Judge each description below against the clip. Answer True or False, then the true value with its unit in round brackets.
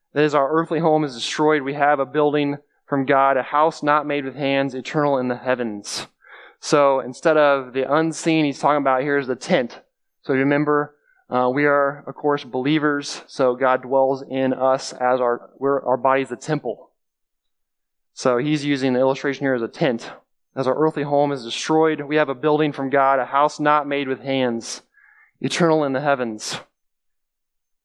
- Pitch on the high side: False (140 Hz)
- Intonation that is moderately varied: False (2.2 semitones)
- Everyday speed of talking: True (185 wpm)